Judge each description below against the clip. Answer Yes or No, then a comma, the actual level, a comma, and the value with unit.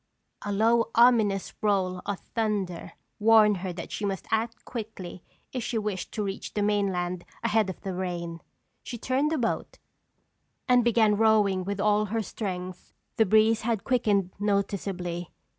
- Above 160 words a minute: No, average, 155 wpm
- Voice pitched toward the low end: No, high, 205 Hz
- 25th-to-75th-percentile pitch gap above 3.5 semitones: No, average, 3.0 semitones